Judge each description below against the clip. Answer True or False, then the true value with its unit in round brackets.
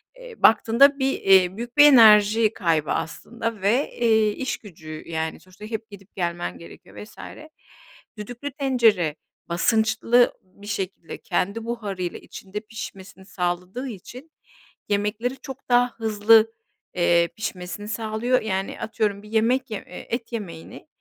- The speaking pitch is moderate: False (215 Hz)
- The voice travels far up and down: False (3.8 semitones)